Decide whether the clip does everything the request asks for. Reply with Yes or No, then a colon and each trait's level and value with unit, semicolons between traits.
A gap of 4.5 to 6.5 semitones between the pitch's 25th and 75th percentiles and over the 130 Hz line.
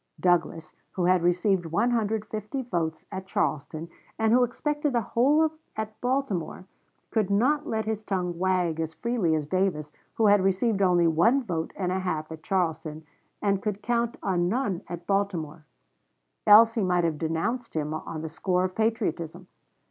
Yes: average, 4.9 semitones; high, 190 Hz